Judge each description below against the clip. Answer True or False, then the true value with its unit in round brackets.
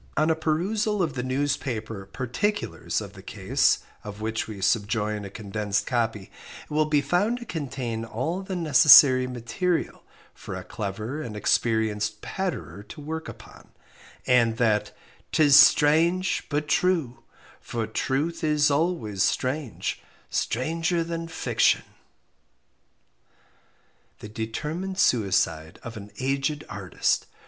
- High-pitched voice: False (130 Hz)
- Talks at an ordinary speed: False (125 wpm)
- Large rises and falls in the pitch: True (6.5 semitones)